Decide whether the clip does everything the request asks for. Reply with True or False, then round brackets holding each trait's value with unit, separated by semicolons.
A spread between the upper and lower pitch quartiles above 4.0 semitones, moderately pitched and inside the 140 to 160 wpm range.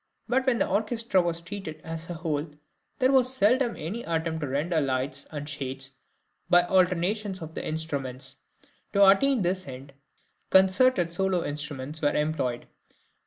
True (5.2 semitones; 170 Hz; 150 wpm)